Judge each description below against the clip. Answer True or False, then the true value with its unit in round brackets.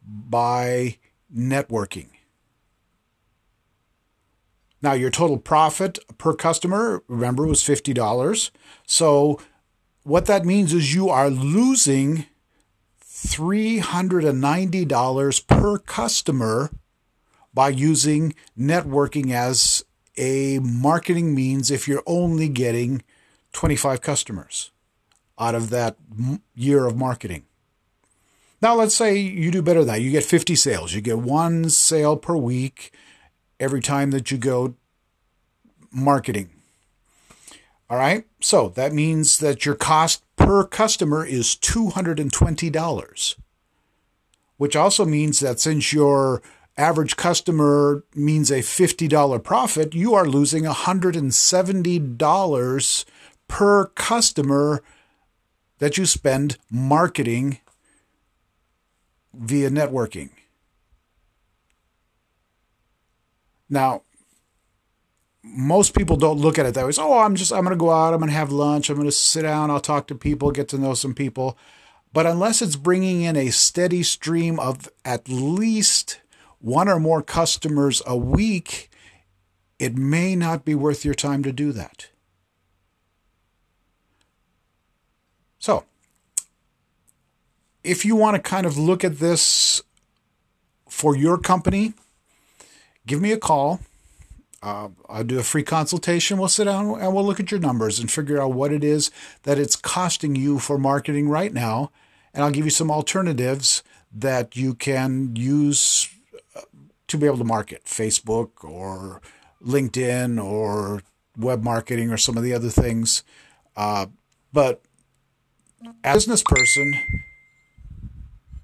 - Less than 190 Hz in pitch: True (140 Hz)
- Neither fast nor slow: False (125 wpm)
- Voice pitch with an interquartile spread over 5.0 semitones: True (5.5 semitones)